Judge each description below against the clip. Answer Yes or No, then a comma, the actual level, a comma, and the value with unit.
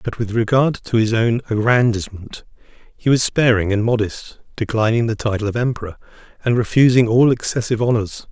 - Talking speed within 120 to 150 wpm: No, average, 160 wpm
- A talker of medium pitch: No, low, 115 Hz